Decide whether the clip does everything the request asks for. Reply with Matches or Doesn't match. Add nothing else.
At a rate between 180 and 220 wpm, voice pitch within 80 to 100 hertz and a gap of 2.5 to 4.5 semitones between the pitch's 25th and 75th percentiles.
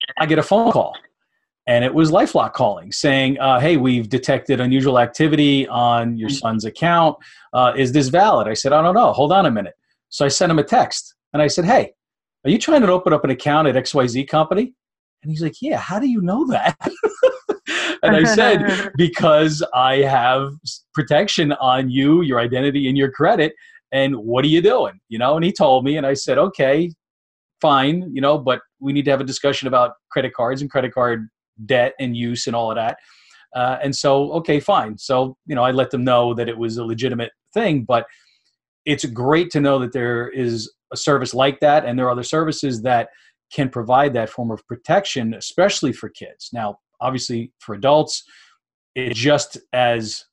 Doesn't match